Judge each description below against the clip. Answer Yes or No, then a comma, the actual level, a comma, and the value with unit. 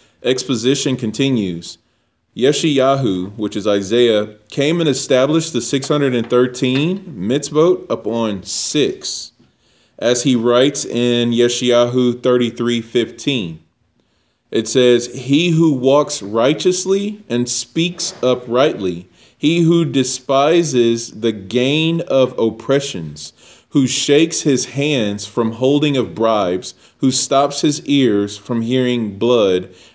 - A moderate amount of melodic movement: Yes, average, 3.7 semitones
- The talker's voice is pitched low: Yes, low, 125 Hz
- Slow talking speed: Yes, slow, 110 wpm